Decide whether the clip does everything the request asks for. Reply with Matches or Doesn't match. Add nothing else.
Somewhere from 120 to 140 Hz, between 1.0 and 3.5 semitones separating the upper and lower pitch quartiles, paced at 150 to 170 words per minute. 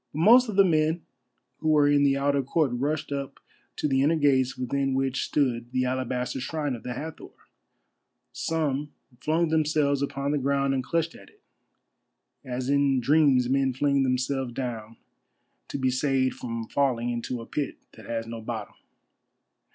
Matches